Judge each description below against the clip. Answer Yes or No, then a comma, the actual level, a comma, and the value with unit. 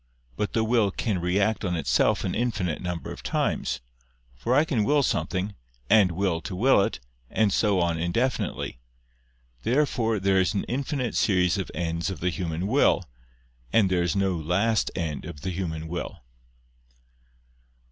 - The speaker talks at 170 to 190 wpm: No, average, 160 wpm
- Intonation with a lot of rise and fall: No, average, 4.3 semitones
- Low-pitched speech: Yes, very low, 95 Hz